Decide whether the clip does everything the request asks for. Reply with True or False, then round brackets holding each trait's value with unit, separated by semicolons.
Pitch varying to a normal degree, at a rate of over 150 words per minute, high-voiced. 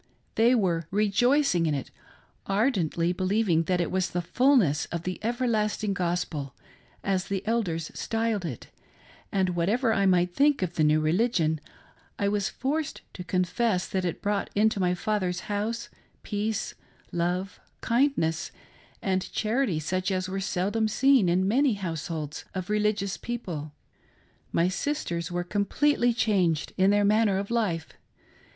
False (4.1 semitones; 145 wpm; 195 Hz)